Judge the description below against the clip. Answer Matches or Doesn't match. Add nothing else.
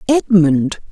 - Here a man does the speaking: Doesn't match